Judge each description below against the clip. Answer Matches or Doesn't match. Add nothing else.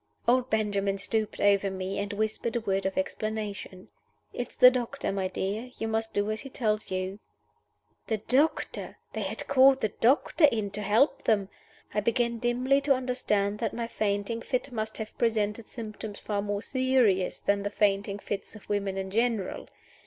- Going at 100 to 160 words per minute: Doesn't match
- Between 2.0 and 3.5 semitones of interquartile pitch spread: Matches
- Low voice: Doesn't match